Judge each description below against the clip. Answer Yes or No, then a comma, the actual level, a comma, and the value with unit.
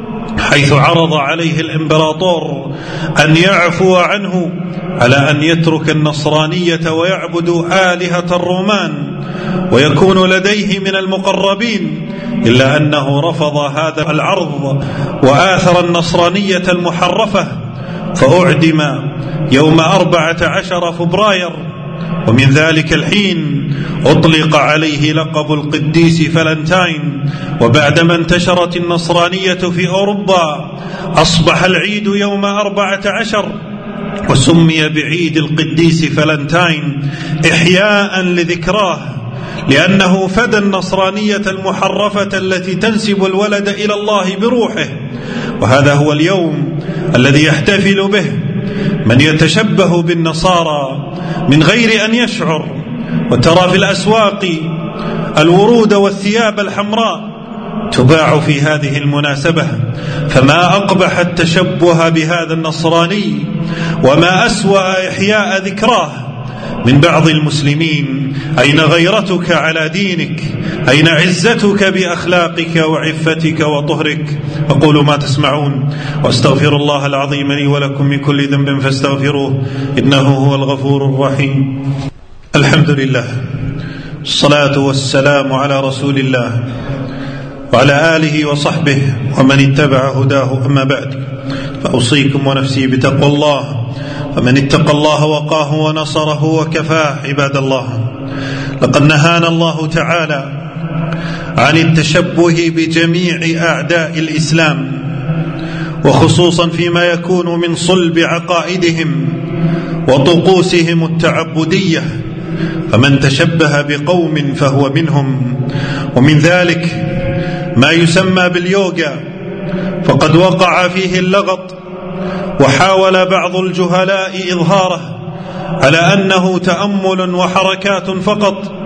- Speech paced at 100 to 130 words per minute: No, average, 90 wpm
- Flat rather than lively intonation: No, average, 3.9 semitones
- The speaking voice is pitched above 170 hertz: No, medium, 165 Hz